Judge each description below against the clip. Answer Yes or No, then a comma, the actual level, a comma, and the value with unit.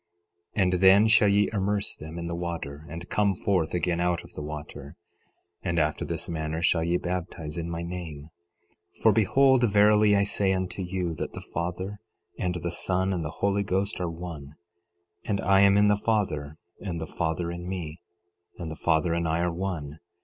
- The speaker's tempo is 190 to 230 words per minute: Yes, average, 195 wpm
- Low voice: Yes, very low, 90 Hz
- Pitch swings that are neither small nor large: Yes, average, 3.1 semitones